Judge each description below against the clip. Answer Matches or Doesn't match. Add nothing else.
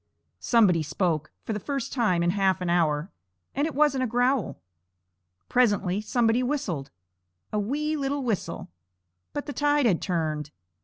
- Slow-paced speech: Doesn't match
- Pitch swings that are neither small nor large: Doesn't match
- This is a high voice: Matches